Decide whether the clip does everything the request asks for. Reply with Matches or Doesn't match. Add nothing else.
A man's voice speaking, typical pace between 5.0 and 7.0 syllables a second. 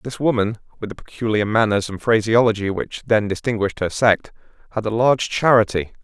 Matches